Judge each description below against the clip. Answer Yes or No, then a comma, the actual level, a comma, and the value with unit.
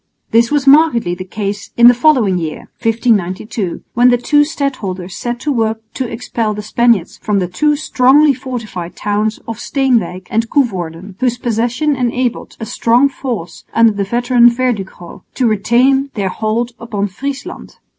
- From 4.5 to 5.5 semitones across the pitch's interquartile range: No, average, 3.9 semitones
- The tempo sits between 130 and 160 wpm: Yes, average, 155 wpm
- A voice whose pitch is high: Yes, high, 230 Hz